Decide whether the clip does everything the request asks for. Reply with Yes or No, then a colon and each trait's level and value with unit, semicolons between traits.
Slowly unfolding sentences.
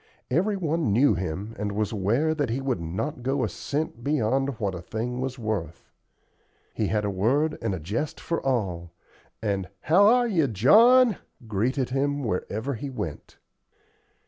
No: average, 165 wpm